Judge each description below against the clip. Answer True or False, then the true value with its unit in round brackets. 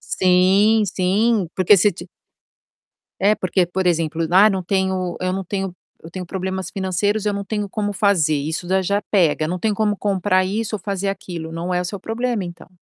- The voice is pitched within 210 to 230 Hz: False (190 Hz)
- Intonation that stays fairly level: True (2.2 semitones)